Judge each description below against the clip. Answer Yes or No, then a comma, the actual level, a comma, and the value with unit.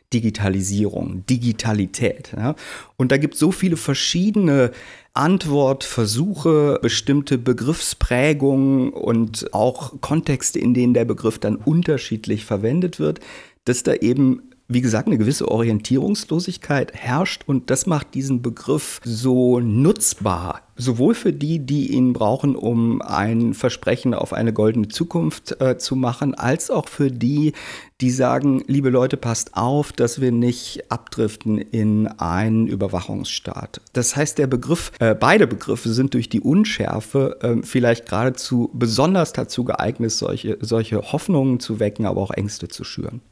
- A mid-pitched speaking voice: No, low, 125 Hz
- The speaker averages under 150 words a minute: Yes, average, 135 wpm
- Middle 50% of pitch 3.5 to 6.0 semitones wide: Yes, average, 4.1 semitones